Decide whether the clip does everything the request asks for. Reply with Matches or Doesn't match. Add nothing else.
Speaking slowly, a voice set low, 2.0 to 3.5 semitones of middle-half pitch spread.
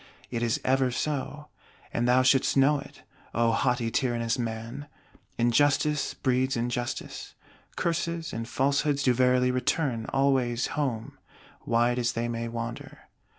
Matches